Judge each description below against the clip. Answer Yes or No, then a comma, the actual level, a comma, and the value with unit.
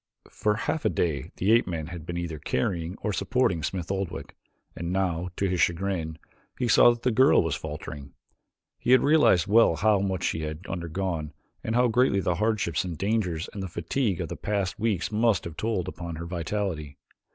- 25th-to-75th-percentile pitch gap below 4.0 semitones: No, average, 4.4 semitones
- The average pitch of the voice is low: Yes, very low, 95 Hz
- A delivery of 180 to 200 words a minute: Yes, average, 195 wpm